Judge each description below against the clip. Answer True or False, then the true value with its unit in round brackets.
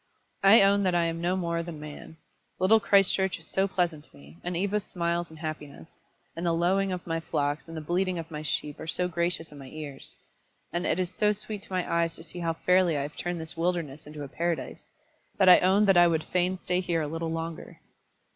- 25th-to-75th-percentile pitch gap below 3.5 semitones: True (2.4 semitones)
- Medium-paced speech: False (230 wpm)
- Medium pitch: True (170 Hz)